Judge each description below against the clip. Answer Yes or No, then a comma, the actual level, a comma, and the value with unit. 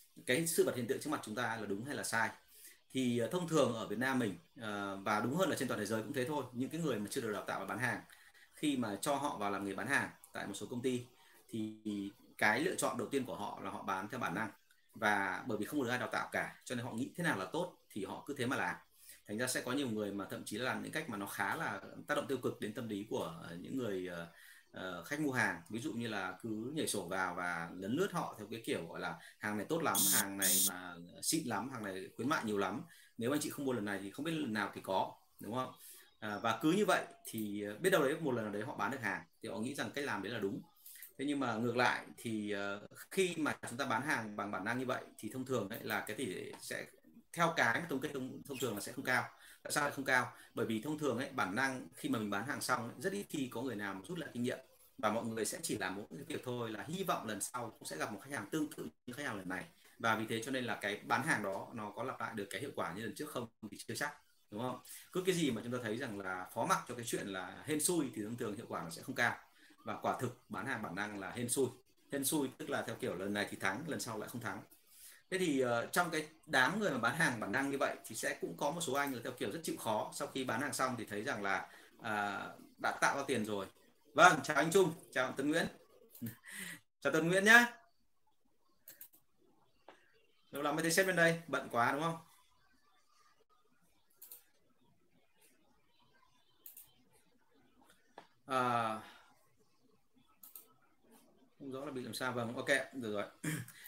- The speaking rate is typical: No, fast, 255 wpm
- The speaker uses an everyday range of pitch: No, wide, 6.4 semitones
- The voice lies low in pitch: Yes, low, 125 Hz